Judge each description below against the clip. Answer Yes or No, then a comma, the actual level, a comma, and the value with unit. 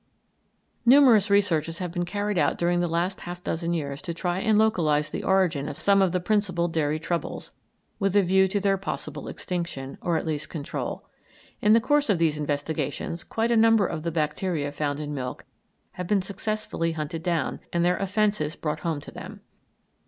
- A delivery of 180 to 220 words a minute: Yes, average, 190 wpm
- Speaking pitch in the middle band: Yes, medium, 175 Hz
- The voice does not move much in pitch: No, average, 4.3 semitones